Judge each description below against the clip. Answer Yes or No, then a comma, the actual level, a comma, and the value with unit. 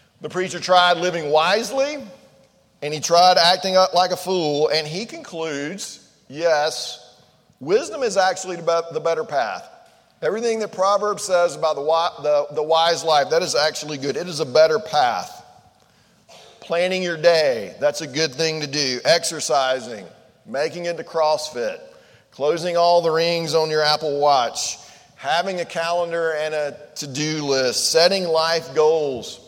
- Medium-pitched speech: Yes, medium, 165 Hz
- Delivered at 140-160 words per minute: Yes, average, 145 wpm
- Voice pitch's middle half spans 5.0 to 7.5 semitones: No, average, 3.0 semitones